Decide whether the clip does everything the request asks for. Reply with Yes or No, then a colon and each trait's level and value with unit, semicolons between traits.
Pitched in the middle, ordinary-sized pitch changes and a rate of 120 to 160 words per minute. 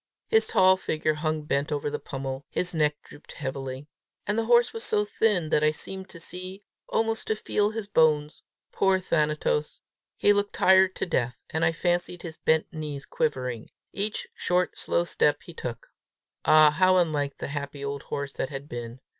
No: medium, 155 Hz; average, 4.6 semitones; average, 180 wpm